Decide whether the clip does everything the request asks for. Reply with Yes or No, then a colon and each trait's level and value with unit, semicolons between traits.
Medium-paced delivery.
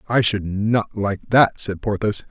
Yes: average, 180 wpm